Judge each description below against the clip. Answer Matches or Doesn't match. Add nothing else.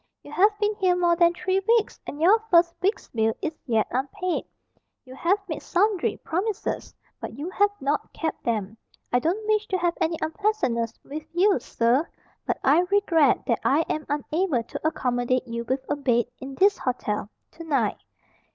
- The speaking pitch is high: Matches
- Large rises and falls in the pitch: Matches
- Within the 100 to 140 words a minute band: Doesn't match